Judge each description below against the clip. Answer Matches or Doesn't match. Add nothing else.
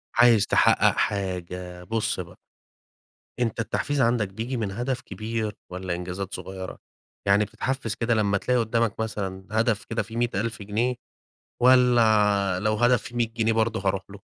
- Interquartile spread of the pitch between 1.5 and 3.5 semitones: Matches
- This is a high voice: Doesn't match